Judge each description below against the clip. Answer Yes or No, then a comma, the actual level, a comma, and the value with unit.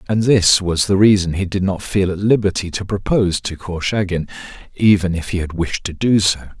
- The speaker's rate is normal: No, fast, 210 wpm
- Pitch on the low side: Yes, very low, 95 Hz